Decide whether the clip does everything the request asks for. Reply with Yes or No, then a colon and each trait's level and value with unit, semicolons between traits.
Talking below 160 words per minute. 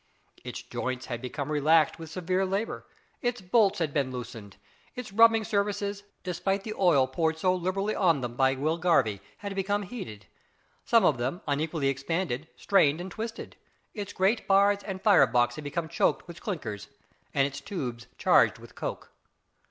No: average, 165 wpm